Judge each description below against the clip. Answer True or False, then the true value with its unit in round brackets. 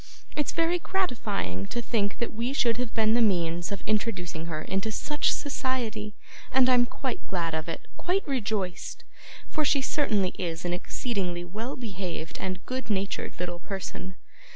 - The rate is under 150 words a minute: False (160 wpm)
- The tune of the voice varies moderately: False (5.8 semitones)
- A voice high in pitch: True (210 Hz)